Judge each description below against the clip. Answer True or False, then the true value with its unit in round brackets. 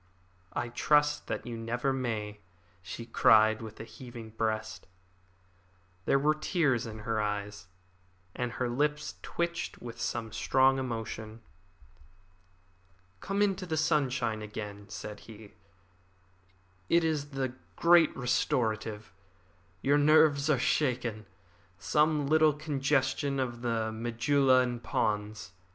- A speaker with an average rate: False (115 wpm)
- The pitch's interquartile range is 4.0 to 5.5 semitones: True (4.7 semitones)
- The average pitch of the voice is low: True (120 Hz)